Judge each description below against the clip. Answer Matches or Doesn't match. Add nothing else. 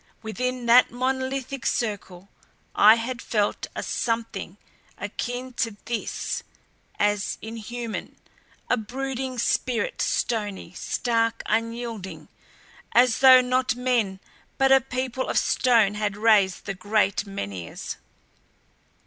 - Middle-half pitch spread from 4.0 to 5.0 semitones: Doesn't match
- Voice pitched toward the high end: Matches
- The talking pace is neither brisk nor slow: Doesn't match